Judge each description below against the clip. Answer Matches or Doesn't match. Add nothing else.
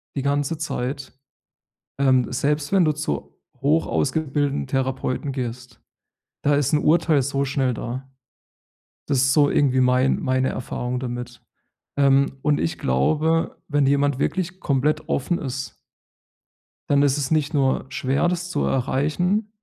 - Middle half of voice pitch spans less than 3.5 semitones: Matches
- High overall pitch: Doesn't match